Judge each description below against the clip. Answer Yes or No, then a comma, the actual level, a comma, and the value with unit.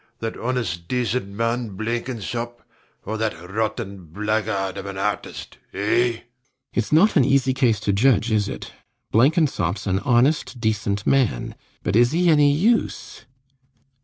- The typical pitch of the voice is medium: No, low, 115 Hz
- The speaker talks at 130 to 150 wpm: Yes, average, 140 wpm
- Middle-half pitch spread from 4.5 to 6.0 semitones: No, average, 4.1 semitones